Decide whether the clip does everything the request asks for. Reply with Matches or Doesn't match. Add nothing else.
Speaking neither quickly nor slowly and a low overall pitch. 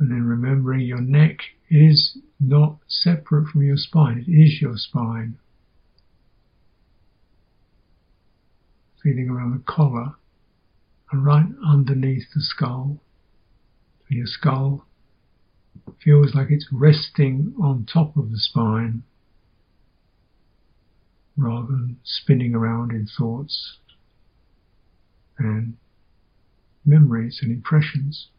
Doesn't match